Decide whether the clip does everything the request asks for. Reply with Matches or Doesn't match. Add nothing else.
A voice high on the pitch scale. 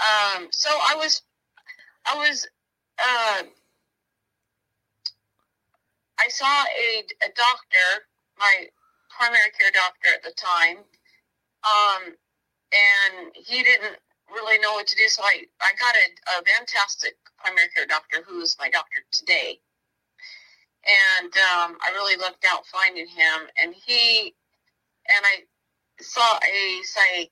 Matches